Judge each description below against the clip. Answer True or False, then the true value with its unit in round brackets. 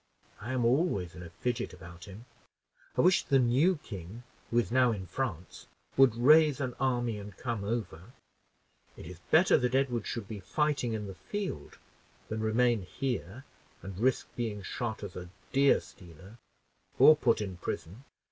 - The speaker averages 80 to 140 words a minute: False (165 wpm)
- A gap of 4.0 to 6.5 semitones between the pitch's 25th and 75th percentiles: True (5.1 semitones)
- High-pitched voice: False (115 Hz)